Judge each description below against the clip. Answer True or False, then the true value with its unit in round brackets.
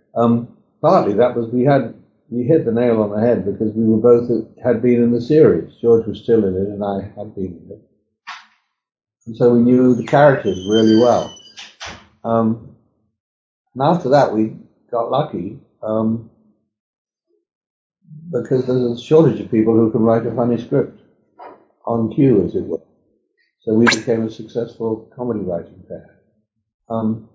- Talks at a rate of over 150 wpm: True (160 wpm)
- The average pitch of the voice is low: True (115 Hz)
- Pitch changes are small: True (1.8 semitones)